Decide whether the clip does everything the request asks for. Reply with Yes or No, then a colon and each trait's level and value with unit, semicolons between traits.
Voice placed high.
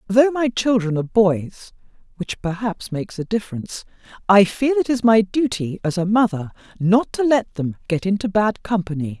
Yes: high, 205 Hz